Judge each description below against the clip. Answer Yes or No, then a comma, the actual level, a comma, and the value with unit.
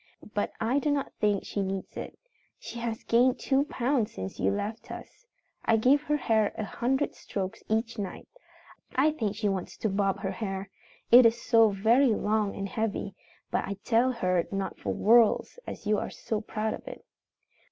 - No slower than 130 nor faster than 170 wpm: No, average, 185 wpm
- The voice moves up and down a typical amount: Yes, average, 3.4 semitones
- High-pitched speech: Yes, high, 220 Hz